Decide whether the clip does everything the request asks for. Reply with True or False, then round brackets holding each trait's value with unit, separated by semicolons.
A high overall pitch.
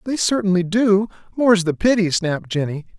True (195 Hz)